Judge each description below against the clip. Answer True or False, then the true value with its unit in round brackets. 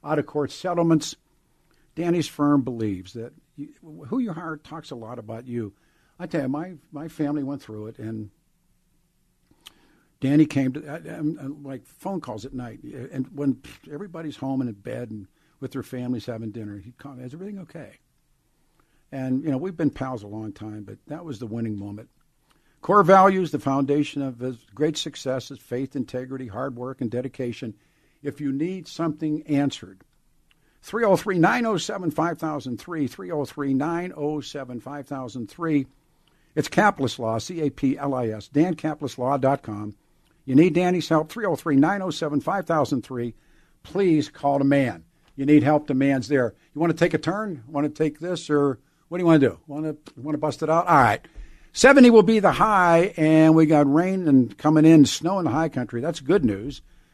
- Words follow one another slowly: False (165 wpm)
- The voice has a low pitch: False (145 Hz)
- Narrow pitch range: False (4.0 semitones)